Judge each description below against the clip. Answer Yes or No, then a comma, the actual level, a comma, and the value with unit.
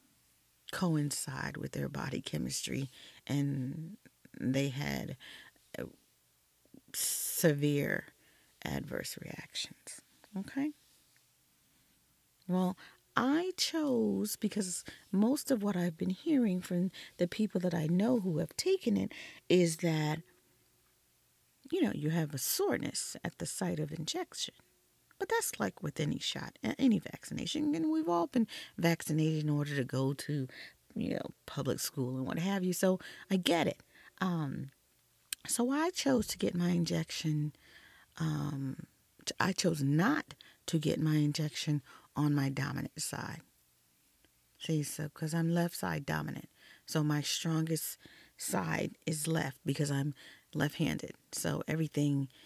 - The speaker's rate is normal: No, slow, 130 wpm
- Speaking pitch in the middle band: Yes, medium, 160 Hz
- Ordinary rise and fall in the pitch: Yes, average, 4.8 semitones